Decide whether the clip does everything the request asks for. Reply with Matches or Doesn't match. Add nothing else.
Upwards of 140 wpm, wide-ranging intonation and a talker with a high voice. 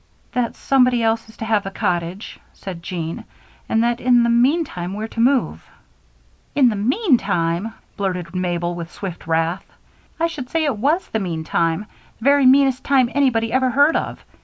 Matches